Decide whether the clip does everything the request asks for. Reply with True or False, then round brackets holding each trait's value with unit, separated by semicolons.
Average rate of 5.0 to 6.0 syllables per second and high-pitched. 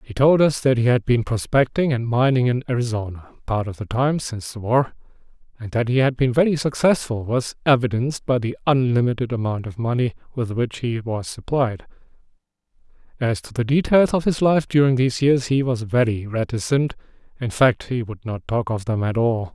False (5.4 syllables/s; 120 Hz)